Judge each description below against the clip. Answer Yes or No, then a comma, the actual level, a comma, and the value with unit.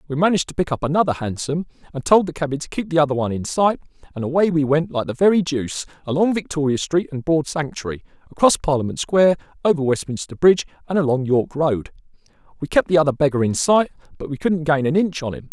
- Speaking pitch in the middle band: Yes, medium, 150 Hz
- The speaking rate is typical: No, fast, 220 wpm